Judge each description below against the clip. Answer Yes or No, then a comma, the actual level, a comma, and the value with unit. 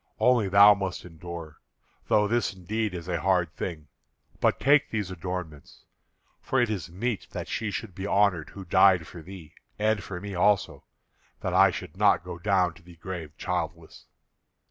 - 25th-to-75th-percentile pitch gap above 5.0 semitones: No, average, 3.4 semitones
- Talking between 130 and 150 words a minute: No, average, 170 wpm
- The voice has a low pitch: Yes, very low, 95 Hz